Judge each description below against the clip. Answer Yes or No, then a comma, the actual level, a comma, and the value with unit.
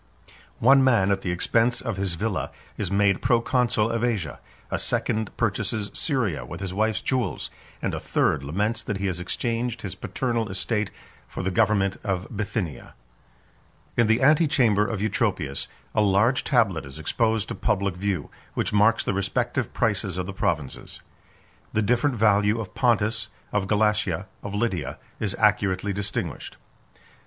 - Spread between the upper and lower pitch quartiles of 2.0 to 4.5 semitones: Yes, average, 3.2 semitones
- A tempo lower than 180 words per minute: Yes, average, 155 wpm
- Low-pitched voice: Yes, low, 105 Hz